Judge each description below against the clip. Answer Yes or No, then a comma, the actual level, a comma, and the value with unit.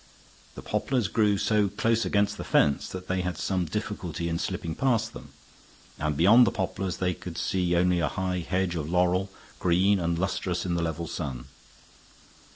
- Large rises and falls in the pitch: No, average, 2.9 semitones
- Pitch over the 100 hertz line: No, very low, 90 Hz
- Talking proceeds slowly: No, average, 175 wpm